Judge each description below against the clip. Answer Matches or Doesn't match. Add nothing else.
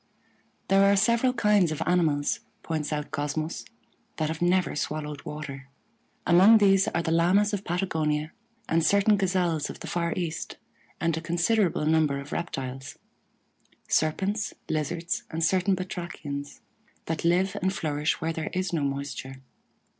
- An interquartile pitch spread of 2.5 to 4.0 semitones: Matches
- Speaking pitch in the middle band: Matches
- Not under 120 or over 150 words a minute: Matches